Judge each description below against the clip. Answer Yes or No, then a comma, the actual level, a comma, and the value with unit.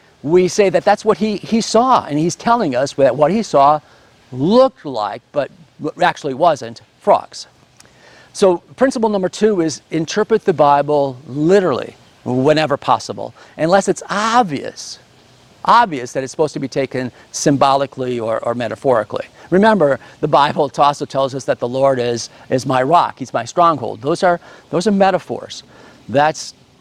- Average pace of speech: Yes, average, 155 wpm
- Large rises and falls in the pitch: Yes, wide, 6.0 semitones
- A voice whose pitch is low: No, medium, 150 Hz